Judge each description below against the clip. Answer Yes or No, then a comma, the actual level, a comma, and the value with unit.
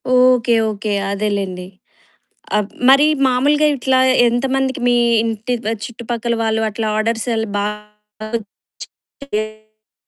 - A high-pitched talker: Yes, high, 225 Hz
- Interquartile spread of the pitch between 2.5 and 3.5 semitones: Yes, average, 3.0 semitones